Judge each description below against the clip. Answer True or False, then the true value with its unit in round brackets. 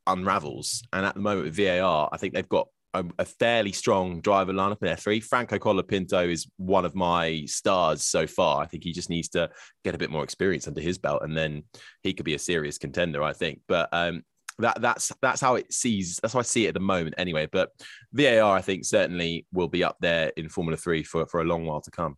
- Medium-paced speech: False (240 wpm)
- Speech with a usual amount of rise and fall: True (3.0 semitones)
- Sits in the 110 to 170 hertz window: False (85 Hz)